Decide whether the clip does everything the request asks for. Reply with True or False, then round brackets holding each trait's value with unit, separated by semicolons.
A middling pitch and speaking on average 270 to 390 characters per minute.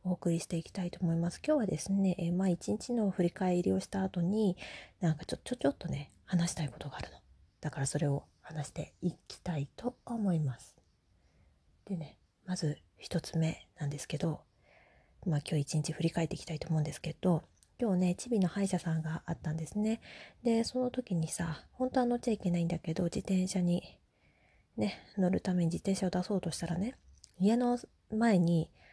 True (175 Hz; 370 characters per minute)